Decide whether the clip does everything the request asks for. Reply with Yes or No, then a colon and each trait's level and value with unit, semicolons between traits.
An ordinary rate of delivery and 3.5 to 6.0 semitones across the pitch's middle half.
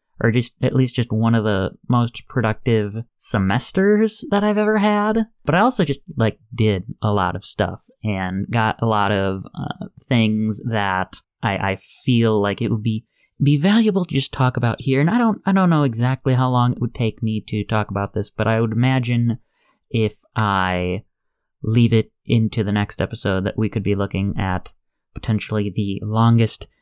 Yes: average, 190 wpm; average, 3.9 semitones